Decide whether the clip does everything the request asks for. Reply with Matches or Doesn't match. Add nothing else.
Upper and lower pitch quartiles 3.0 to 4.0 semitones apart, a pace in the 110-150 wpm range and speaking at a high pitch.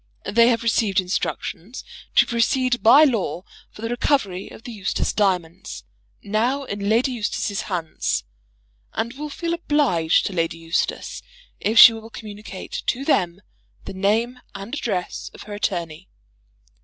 Doesn't match